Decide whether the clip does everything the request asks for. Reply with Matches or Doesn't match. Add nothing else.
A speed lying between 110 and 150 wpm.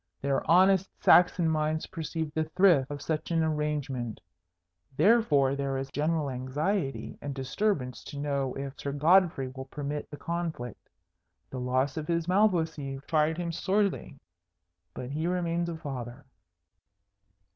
Matches